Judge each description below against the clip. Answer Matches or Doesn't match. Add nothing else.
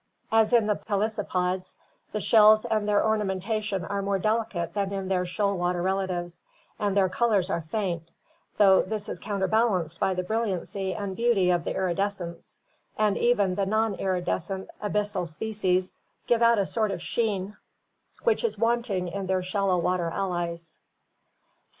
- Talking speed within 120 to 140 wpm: Doesn't match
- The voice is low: Doesn't match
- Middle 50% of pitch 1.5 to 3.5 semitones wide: Matches